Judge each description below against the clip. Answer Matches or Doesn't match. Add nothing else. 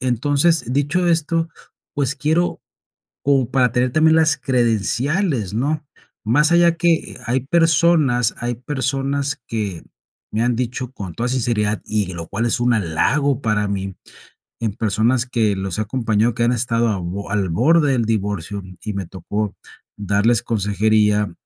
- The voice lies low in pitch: Matches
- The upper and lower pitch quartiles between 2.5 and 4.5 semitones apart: Doesn't match